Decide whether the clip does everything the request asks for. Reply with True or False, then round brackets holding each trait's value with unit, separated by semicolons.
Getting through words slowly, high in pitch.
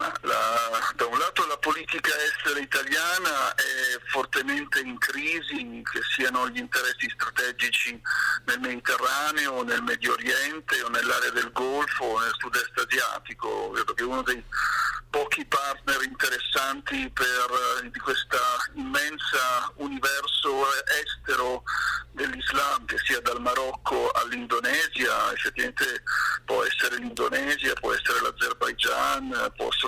True (110 wpm; 370 Hz)